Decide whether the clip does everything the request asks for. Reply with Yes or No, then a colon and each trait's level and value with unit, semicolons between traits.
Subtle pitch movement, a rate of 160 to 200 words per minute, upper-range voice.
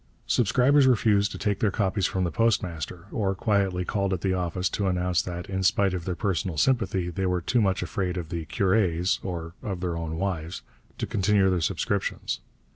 No: narrow, 2.3 semitones; average, 195 wpm; very low, 95 Hz